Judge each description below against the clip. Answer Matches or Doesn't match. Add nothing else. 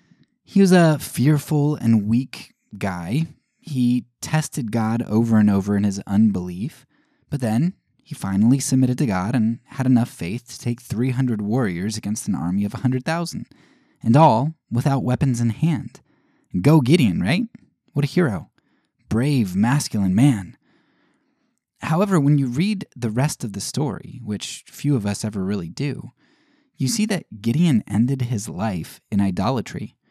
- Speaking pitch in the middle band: Doesn't match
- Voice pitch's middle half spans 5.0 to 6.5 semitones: Matches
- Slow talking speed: Doesn't match